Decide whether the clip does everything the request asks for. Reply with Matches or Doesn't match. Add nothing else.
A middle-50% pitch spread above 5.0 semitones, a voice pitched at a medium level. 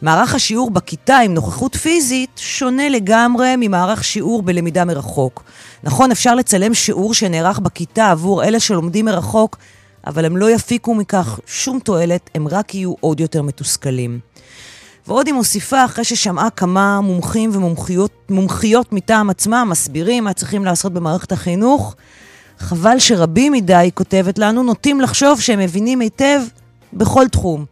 Doesn't match